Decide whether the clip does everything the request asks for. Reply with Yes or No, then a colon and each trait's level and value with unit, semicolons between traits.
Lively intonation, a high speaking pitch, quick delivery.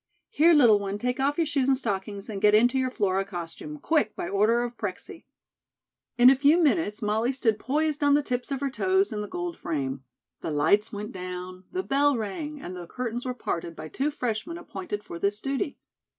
Yes: wide, 6.1 semitones; high, 240 Hz; fast, 210 wpm